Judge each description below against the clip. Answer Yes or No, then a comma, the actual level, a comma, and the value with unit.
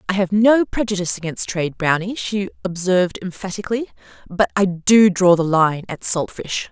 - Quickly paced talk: No, average, 170 wpm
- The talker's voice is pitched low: No, high, 190 Hz